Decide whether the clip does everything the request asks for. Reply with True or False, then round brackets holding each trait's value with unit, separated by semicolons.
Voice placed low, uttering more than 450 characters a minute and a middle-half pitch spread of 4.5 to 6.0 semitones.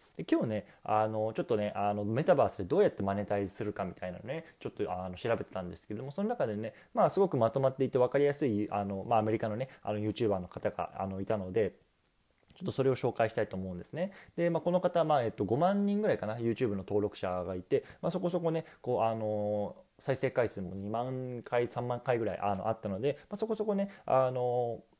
True (115 Hz; 470 characters per minute; 5.3 semitones)